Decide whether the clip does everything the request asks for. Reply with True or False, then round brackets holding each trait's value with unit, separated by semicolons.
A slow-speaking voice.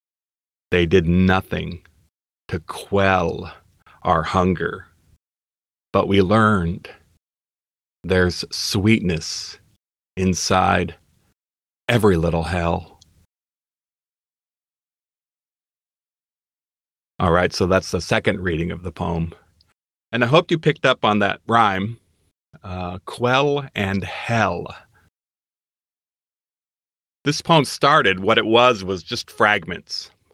True (95 wpm)